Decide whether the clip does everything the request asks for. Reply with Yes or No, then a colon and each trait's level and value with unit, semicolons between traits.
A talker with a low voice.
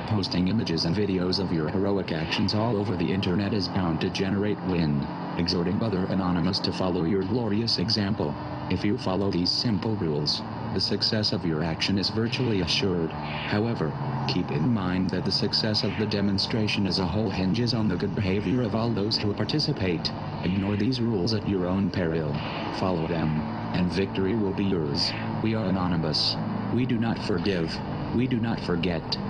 Yes: low, 100 Hz